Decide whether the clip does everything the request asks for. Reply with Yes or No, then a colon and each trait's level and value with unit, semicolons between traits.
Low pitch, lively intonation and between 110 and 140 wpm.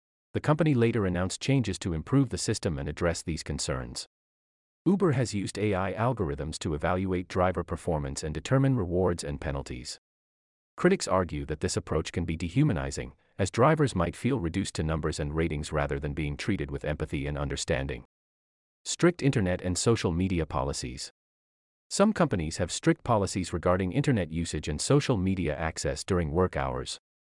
No: very low, 90 Hz; wide, 5.8 semitones; average, 160 wpm